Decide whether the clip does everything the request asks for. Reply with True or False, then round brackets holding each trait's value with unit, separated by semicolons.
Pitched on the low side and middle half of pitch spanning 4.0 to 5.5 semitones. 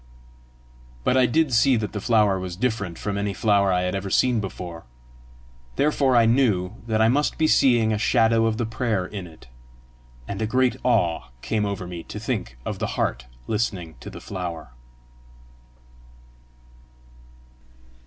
True (105 Hz; 4.3 semitones)